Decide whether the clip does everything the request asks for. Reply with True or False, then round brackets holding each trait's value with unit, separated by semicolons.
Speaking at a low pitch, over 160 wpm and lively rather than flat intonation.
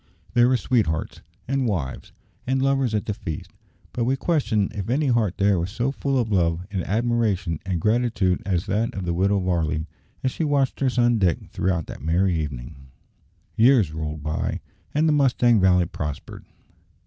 True (100 Hz; 175 wpm; 6.3 semitones)